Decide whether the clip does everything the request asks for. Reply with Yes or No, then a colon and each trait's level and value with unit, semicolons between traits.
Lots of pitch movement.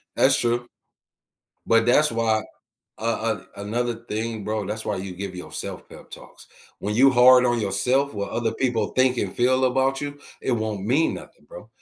No: average, 3.2 semitones